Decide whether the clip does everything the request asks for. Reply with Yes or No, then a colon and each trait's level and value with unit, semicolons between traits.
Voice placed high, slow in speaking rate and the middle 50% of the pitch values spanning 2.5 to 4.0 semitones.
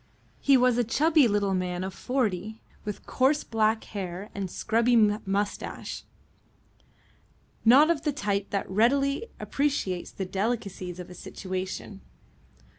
No: high, 210 Hz; slow, 125 wpm; average, 4.8 semitones